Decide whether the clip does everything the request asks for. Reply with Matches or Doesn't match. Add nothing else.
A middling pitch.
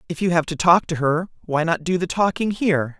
Matches